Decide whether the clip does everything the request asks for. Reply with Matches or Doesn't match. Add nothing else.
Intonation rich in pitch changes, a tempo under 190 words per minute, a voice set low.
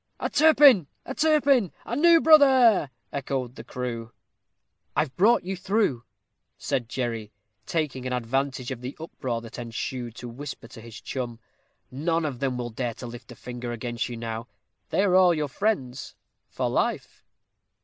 Matches